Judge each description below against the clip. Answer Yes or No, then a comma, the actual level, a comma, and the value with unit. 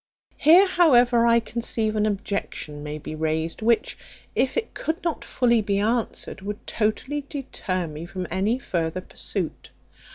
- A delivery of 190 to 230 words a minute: No, average, 150 wpm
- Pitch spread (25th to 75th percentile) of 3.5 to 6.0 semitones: Yes, average, 5.1 semitones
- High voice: Yes, high, 215 Hz